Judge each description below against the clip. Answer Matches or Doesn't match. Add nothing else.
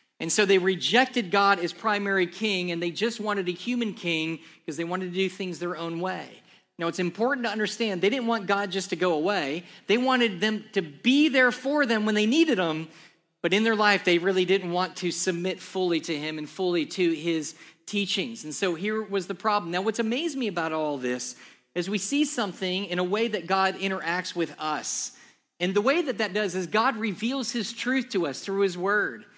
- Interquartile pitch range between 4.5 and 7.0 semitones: Doesn't match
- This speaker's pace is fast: Matches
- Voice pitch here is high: Matches